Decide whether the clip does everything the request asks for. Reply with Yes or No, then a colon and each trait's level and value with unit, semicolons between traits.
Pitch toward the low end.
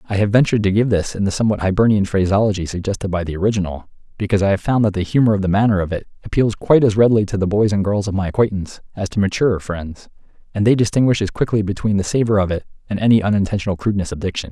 Yes: low, 100 Hz